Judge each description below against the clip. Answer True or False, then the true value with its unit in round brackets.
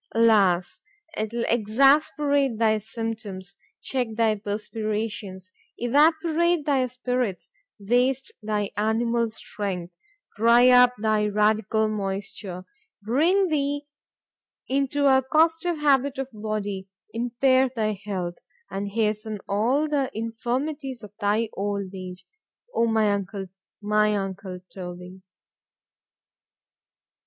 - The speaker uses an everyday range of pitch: True (4.4 semitones)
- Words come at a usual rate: False (90 wpm)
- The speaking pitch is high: True (220 Hz)